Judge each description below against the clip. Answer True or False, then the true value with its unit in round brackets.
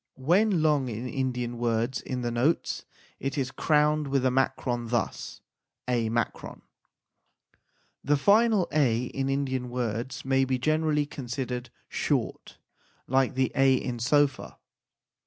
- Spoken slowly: True (125 wpm)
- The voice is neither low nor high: False (130 Hz)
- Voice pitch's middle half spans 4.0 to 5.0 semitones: False (3.1 semitones)